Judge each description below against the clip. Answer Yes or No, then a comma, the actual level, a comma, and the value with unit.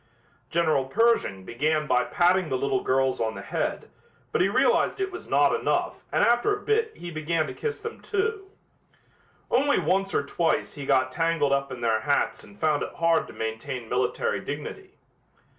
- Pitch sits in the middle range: Yes, medium, 155 Hz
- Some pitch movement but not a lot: No, wide, 7.7 semitones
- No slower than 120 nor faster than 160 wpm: No, average, 180 wpm